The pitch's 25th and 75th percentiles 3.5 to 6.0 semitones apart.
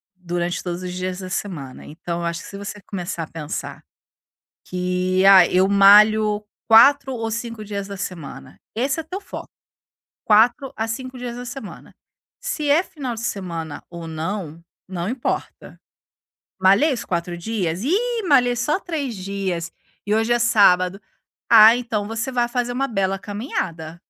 Yes: average, 5.0 semitones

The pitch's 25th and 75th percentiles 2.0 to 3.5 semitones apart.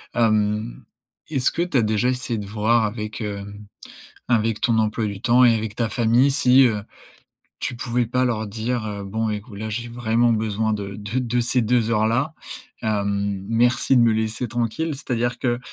Yes: narrow, 2.4 semitones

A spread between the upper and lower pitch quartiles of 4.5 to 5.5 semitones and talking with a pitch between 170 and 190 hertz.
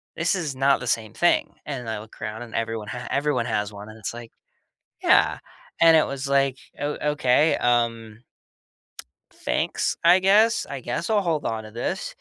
No: average, 4.9 semitones; low, 125 Hz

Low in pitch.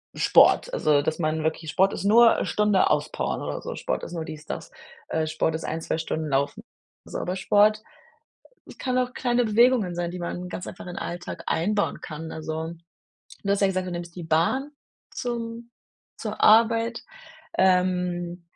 No: medium, 180 Hz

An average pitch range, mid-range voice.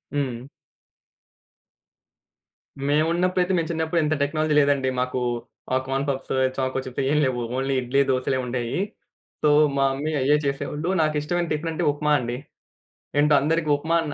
Yes: average, 3.0 semitones; medium, 145 Hz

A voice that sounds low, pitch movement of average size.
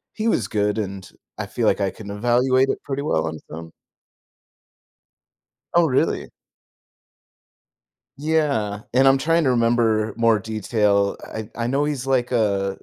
Yes: low, 115 Hz; average, 4.6 semitones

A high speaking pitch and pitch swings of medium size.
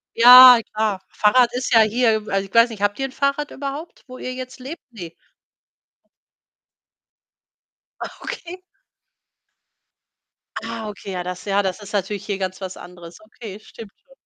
Yes: high, 220 Hz; average, 4.5 semitones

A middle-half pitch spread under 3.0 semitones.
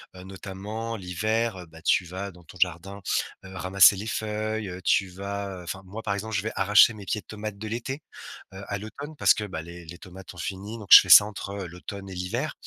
Yes: narrow, 2.6 semitones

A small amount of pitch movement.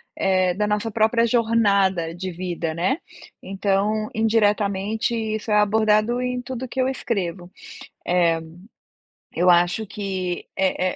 No: average, 3.4 semitones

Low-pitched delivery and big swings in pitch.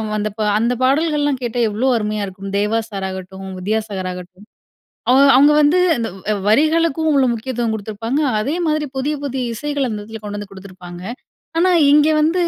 No: high, 225 Hz; wide, 5.9 semitones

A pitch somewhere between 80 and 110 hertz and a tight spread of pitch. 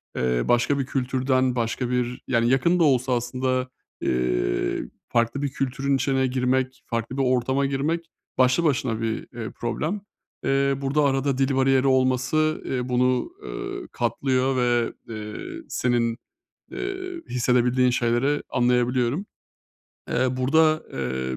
No: low, 130 Hz; narrow, 2.1 semitones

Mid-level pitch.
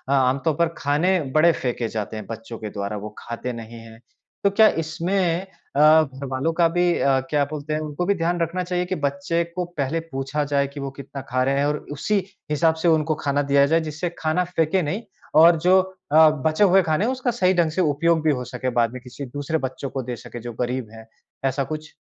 Yes: medium, 150 Hz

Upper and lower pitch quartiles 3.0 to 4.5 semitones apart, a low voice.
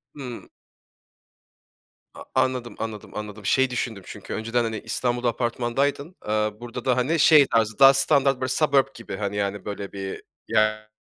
Yes: average, 3.6 semitones; low, 120 Hz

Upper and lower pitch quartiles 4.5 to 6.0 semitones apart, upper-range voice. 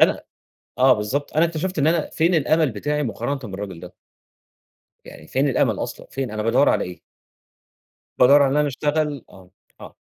No: average, 5.0 semitones; medium, 140 Hz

